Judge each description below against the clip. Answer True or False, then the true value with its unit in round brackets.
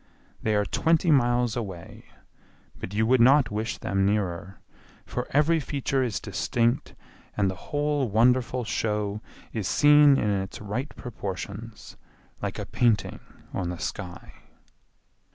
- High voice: False (115 Hz)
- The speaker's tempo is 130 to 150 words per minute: True (135 wpm)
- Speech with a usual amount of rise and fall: True (4.5 semitones)